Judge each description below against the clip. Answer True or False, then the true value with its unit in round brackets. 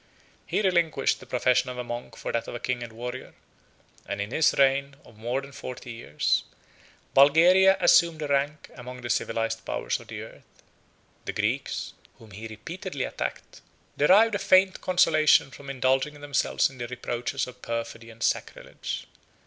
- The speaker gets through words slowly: False (165 wpm)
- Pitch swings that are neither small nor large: True (4.3 semitones)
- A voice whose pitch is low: True (130 Hz)